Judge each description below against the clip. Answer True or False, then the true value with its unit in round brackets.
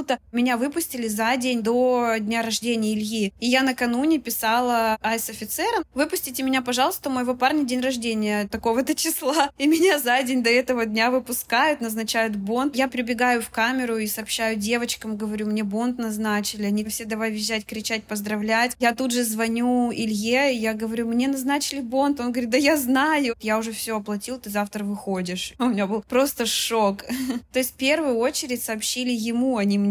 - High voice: True (240 Hz)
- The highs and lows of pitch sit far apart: False (2.7 semitones)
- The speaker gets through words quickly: True (175 wpm)